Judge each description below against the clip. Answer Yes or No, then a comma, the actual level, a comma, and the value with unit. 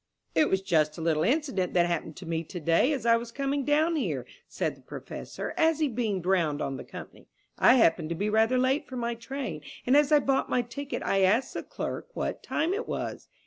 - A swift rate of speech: Yes, fast, 225 wpm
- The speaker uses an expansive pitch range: Yes, wide, 8.2 semitones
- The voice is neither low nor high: No, high, 230 Hz